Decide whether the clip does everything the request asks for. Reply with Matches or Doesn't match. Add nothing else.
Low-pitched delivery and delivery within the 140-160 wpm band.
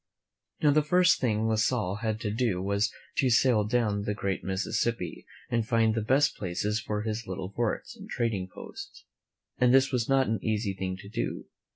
Doesn't match